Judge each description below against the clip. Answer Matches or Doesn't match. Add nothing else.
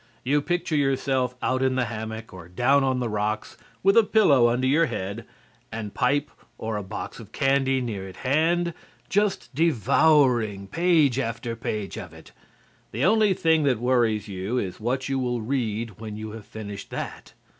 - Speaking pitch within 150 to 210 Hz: Doesn't match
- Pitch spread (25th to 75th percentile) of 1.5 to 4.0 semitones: Doesn't match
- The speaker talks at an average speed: Matches